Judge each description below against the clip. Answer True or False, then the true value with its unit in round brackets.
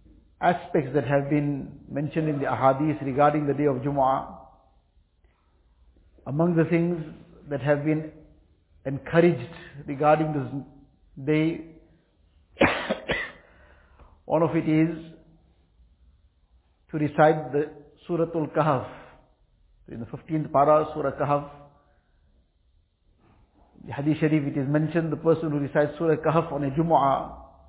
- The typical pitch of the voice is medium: True (145 Hz)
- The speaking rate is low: True (115 wpm)